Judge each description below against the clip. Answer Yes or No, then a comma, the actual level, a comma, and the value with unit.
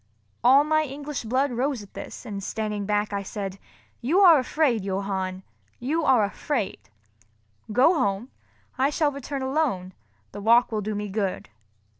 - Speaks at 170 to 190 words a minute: No, average, 150 wpm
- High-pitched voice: Yes, high, 235 Hz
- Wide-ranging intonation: Yes, wide, 5.7 semitones